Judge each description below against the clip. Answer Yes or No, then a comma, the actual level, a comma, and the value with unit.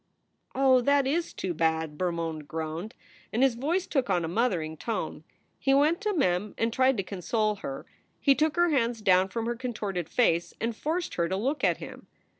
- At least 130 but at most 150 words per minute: No, average, 195 wpm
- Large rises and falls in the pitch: Yes, wide, 7.4 semitones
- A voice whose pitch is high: Yes, high, 225 Hz